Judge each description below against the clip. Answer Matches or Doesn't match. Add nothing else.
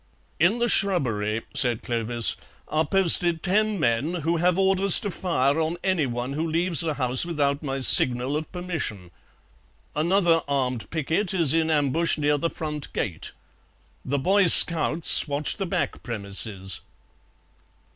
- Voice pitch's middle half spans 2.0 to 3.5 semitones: Doesn't match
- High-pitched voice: Doesn't match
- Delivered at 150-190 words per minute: Doesn't match